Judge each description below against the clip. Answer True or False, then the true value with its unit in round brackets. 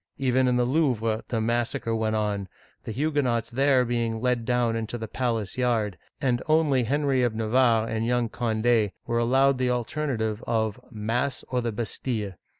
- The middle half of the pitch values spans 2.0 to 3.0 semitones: True (2.4 semitones)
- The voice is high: False (120 Hz)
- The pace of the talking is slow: False (165 wpm)